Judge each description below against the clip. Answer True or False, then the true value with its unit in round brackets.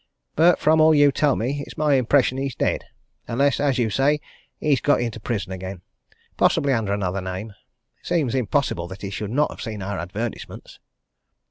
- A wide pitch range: True (6.0 semitones)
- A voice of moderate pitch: False (120 Hz)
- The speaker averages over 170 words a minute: True (180 wpm)